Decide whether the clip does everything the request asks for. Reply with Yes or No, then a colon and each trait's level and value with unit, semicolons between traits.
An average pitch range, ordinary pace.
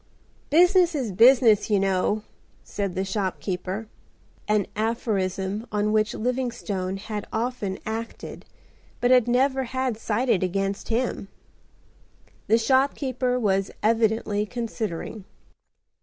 No: average, 3.9 semitones; slow, 100 wpm